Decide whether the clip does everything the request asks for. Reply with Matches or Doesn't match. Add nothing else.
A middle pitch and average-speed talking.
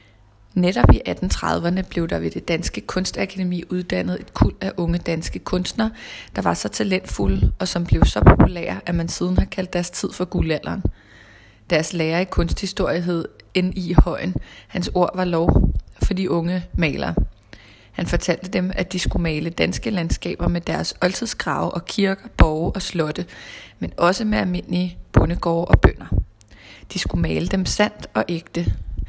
Matches